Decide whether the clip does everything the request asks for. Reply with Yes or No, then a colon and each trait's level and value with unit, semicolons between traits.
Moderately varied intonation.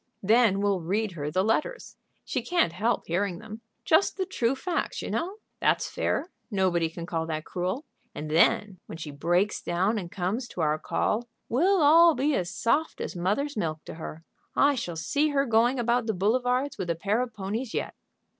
No: wide, 6.4 semitones